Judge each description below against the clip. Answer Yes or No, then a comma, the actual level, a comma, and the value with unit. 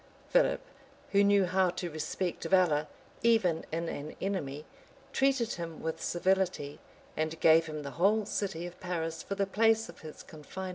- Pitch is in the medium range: Yes, medium, 175 Hz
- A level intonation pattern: No, average, 3.8 semitones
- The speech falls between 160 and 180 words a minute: Yes, average, 170 wpm